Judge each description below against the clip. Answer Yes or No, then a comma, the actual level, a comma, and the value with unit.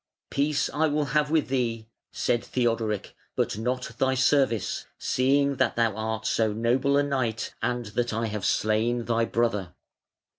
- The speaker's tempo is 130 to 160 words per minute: Yes, average, 155 wpm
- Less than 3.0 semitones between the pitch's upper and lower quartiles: No, average, 3.4 semitones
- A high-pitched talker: No, low, 120 Hz